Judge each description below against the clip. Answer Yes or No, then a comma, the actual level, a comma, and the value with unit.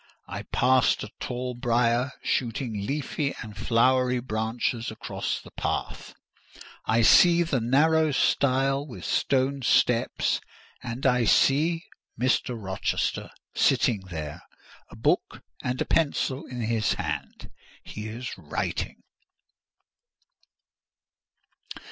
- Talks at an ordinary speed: No, slow, 105 wpm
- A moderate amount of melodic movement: Yes, average, 3.1 semitones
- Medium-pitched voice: No, low, 125 Hz